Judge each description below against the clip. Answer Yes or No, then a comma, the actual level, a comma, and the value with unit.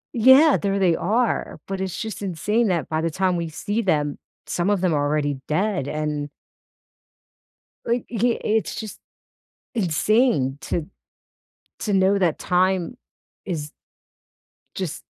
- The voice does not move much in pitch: No, average, 5.3 semitones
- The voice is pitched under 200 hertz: Yes, medium, 185 Hz